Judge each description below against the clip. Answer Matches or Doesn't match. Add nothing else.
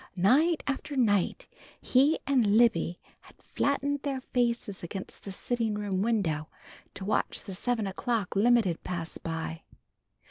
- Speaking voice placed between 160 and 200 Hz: Doesn't match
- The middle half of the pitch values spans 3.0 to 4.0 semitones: Doesn't match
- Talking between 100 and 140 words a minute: Matches